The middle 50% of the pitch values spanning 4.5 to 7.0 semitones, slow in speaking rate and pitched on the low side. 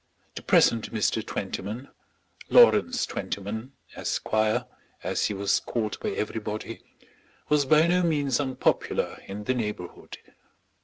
Yes: average, 5.1 semitones; slow, 115 wpm; low, 110 Hz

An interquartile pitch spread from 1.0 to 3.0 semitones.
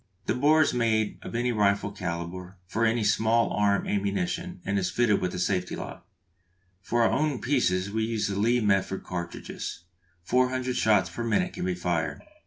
No: average, 4.3 semitones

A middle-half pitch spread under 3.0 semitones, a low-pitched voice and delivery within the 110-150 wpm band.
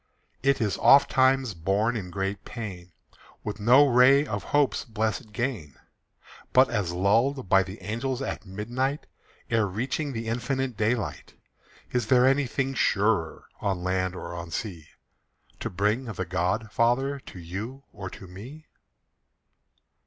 No: average, 5.3 semitones; low, 110 Hz; average, 140 wpm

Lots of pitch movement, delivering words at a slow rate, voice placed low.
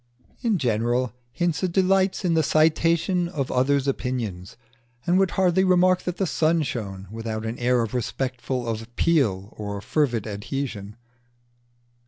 Yes: wide, 7.3 semitones; slow, 130 wpm; low, 130 Hz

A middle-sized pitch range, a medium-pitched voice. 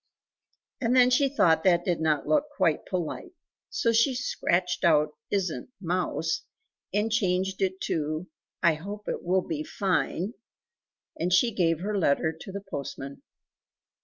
Yes: average, 4.2 semitones; medium, 180 Hz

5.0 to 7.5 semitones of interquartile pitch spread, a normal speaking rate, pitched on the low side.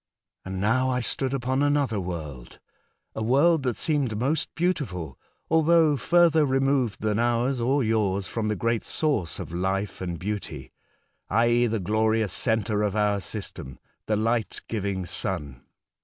Yes: average, 5.3 semitones; average, 155 wpm; low, 110 Hz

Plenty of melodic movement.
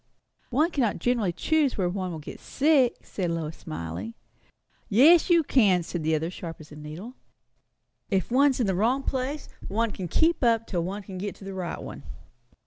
Yes: wide, 7.1 semitones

